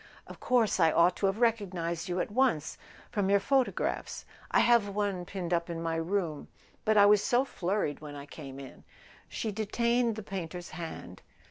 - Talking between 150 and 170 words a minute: No, average, 185 wpm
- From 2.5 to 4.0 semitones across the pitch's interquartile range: No, average, 4.5 semitones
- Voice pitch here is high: Yes, high, 195 Hz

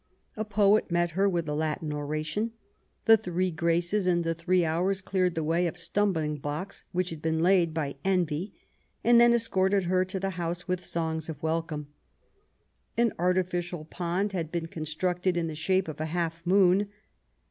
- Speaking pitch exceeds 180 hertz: No, medium, 175 Hz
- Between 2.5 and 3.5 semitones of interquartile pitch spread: Yes, average, 2.8 semitones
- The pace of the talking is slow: No, average, 175 wpm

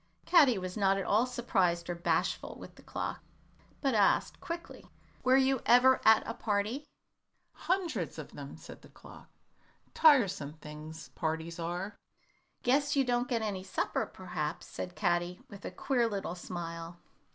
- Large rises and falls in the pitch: Yes, wide, 6.4 semitones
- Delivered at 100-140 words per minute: No, average, 150 wpm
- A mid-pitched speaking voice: No, high, 200 Hz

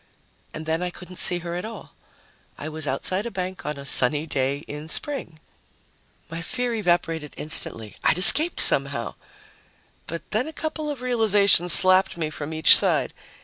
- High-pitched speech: No, medium, 170 Hz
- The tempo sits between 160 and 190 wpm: Yes, average, 165 wpm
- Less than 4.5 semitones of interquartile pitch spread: No, average, 5.2 semitones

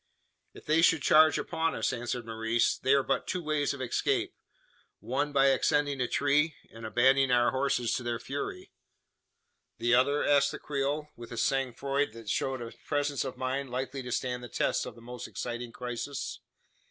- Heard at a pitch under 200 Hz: Yes, low, 135 Hz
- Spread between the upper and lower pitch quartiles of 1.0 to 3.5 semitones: Yes, average, 2.9 semitones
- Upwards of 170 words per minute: Yes, average, 185 wpm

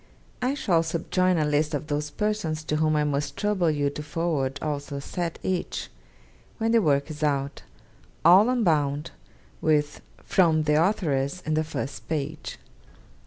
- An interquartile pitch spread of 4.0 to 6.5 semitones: No, average, 3.1 semitones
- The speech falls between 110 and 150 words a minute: No, average, 160 wpm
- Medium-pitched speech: Yes, medium, 155 Hz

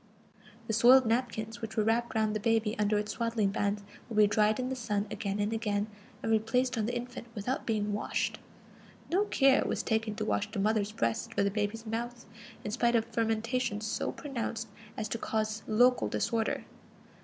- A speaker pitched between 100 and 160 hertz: No, high, 220 Hz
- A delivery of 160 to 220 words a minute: Yes, average, 190 wpm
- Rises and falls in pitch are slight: Yes, narrow, 2.0 semitones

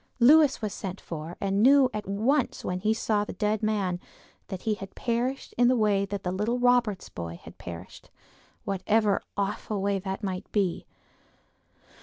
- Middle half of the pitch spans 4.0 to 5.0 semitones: No, average, 3.2 semitones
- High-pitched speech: Yes, high, 205 Hz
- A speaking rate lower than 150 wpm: No, average, 165 wpm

